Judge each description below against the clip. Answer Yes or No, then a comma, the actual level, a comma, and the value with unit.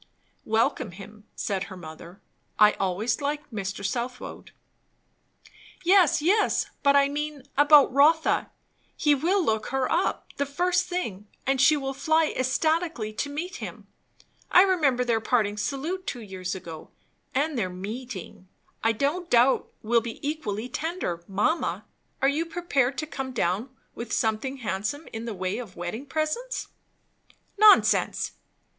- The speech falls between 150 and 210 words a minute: No, average, 140 wpm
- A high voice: Yes, very high, 260 Hz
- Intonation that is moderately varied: No, wide, 6.3 semitones